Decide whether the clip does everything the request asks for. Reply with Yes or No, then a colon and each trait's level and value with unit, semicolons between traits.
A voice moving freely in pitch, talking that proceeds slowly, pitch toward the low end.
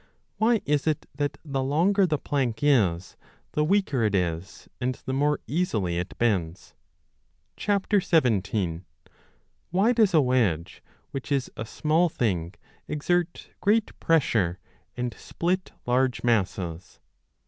Yes: wide, 8.7 semitones; slow, 125 wpm; low, 130 Hz